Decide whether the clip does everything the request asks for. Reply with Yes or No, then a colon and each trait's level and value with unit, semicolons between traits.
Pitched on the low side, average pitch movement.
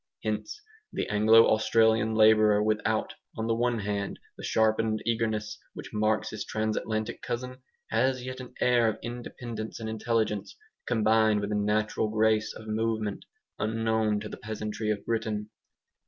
No: low, 110 Hz; narrow, 1.0 semitones